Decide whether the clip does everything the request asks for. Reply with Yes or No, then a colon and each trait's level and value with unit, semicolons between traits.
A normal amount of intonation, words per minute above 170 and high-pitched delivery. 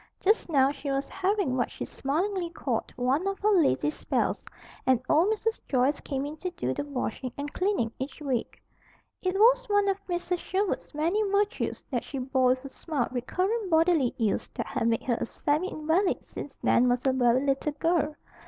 No: wide, 6.2 semitones; average, 190 wpm; very high, 300 Hz